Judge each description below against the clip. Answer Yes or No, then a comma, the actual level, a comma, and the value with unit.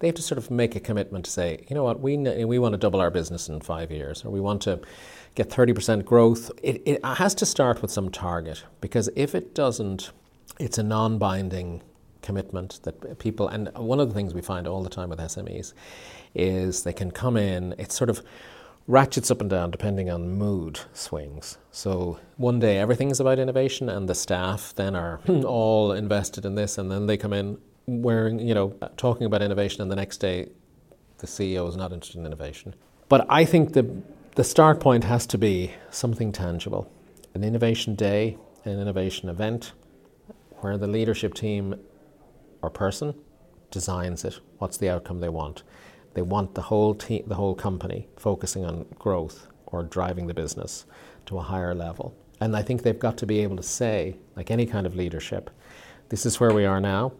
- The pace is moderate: Yes, average, 195 wpm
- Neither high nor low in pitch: No, low, 100 Hz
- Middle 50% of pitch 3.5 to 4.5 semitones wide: Yes, average, 4.1 semitones